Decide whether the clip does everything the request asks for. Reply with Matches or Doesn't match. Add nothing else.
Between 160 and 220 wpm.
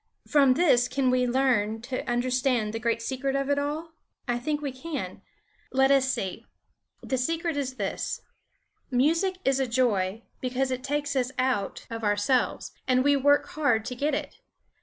Matches